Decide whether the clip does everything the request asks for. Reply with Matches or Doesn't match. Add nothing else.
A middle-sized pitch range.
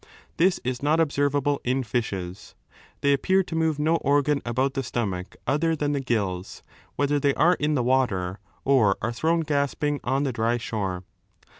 Matches